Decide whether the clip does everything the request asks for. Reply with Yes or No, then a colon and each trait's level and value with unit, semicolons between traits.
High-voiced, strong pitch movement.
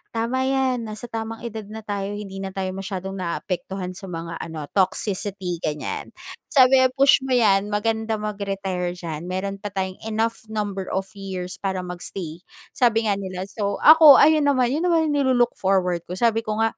No: high, 200 Hz; average, 3.4 semitones